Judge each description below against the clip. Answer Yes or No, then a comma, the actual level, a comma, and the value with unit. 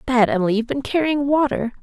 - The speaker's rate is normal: Yes, average, 195 wpm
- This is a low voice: No, very high, 250 Hz